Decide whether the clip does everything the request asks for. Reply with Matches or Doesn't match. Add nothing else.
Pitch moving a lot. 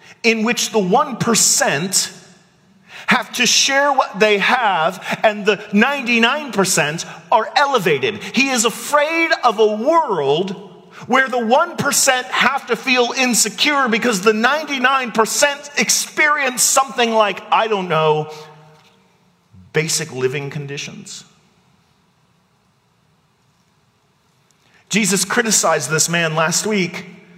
Matches